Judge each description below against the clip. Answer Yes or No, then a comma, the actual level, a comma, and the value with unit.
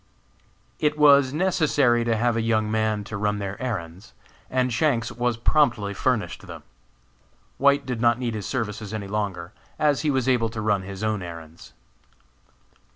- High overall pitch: No, low, 115 Hz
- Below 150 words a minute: No, average, 160 wpm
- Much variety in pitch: No, average, 3.8 semitones